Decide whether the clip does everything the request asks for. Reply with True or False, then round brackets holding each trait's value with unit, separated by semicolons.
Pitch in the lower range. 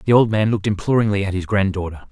True (100 Hz)